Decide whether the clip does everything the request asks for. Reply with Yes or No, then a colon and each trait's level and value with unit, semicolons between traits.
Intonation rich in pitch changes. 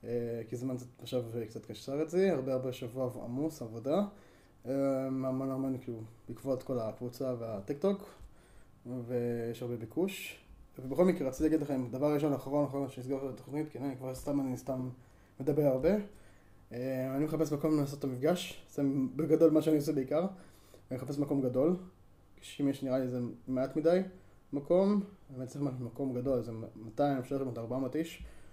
No: average, 3.5 semitones